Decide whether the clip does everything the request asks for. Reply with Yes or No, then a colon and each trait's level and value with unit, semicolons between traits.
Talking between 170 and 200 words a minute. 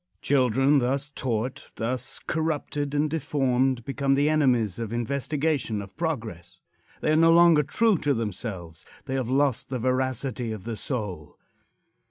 No: average, 145 wpm